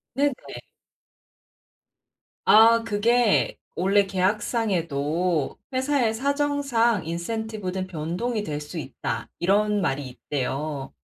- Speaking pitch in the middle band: No, high, 200 Hz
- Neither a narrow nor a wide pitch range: No, wide, 6.3 semitones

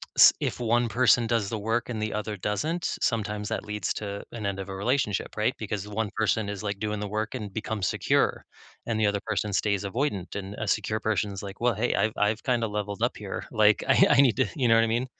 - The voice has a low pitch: Yes, low, 105 Hz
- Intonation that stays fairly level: Yes, narrow, 2.0 semitones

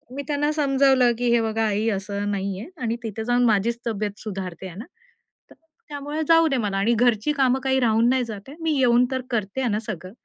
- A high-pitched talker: Yes, high, 235 Hz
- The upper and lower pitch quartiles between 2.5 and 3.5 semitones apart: No, average, 4.2 semitones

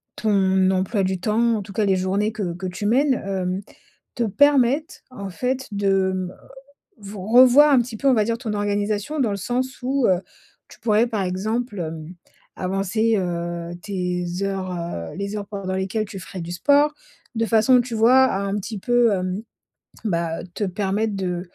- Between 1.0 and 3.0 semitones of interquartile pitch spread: No, average, 3.7 semitones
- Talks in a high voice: Yes, high, 205 Hz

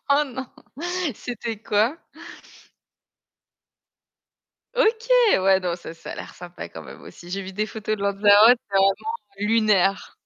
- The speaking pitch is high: Yes, high, 210 Hz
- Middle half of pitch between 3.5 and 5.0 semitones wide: Yes, average, 4.0 semitones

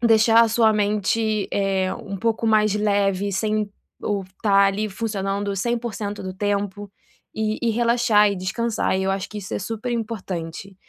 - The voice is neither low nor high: No, high, 205 Hz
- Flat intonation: Yes, narrow, 2.1 semitones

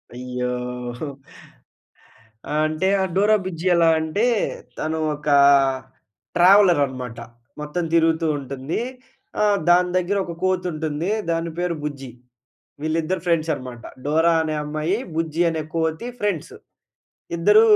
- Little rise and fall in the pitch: No, average, 3.3 semitones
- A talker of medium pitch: Yes, medium, 160 Hz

